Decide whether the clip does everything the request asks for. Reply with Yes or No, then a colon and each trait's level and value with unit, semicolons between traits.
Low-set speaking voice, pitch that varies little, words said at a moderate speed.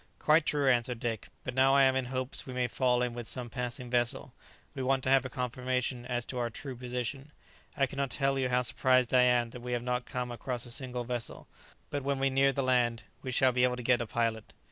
No: low, 125 Hz; narrow, 1.5 semitones; fast, 245 wpm